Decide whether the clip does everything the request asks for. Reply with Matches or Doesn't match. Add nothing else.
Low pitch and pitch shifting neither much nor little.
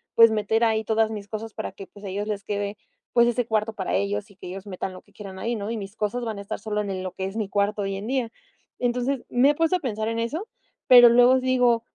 Doesn't match